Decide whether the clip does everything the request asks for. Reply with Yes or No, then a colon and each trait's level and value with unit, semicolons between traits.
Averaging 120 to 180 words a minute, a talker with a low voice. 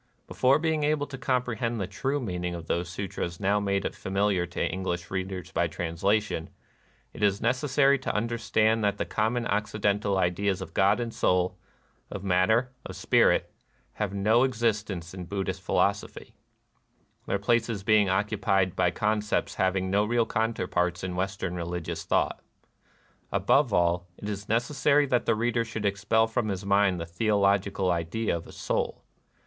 Yes: average, 160 wpm; low, 100 Hz